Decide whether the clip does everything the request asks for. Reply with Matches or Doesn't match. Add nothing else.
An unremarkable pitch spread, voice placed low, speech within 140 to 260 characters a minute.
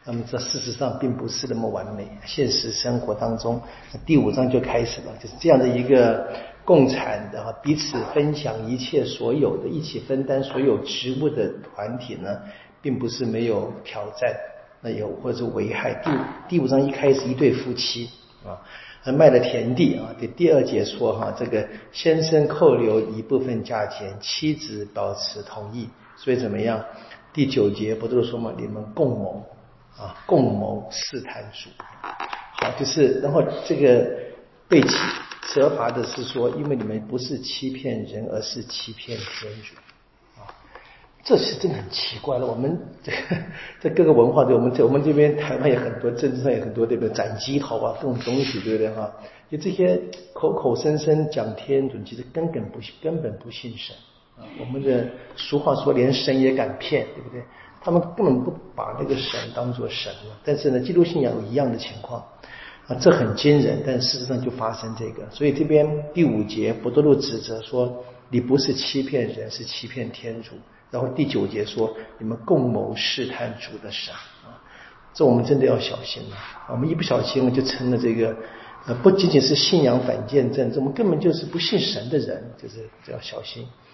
Doesn't match